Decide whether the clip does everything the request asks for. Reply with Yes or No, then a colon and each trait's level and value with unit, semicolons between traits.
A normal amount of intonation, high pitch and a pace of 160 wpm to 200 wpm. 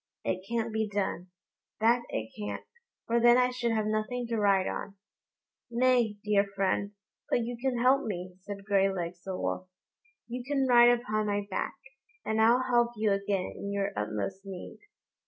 Yes: average, 3.4 semitones; high, 215 Hz; average, 170 wpm